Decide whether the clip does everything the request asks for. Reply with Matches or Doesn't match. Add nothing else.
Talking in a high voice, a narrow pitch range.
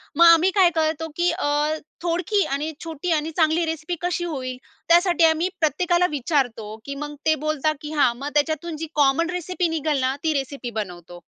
Doesn't match